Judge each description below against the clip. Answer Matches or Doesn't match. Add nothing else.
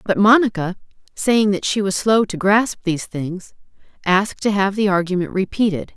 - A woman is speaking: Matches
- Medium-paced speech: Matches